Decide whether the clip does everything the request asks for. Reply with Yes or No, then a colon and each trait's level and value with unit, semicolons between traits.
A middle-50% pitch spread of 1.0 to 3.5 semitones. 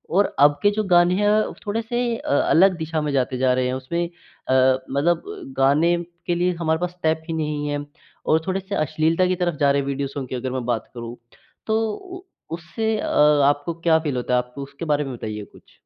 No: average, 4.7 semitones